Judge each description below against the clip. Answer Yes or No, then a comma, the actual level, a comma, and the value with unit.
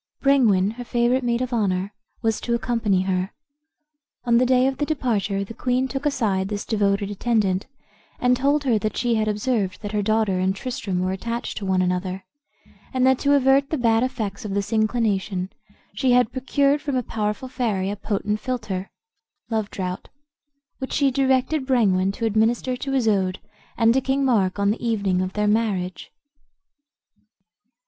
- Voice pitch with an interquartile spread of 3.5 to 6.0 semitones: Yes, average, 4.4 semitones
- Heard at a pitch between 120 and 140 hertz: No, high, 225 Hz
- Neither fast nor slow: Yes, average, 170 wpm